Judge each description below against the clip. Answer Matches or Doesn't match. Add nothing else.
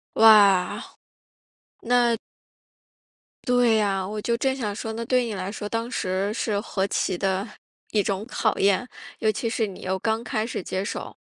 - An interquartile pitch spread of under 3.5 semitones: Matches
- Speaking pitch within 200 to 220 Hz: Matches